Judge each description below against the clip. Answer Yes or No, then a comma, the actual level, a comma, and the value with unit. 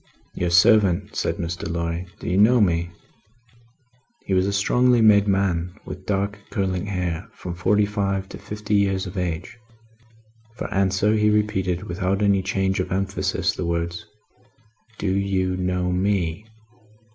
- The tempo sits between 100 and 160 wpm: Yes, average, 145 wpm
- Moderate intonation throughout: No, narrow, 2.2 semitones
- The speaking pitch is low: Yes, very low, 95 Hz